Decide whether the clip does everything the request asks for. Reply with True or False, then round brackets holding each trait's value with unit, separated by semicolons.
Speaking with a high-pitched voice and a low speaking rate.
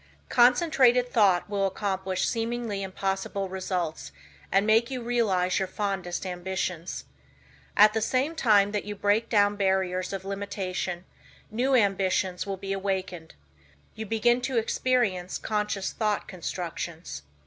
True (200 Hz; 125 wpm)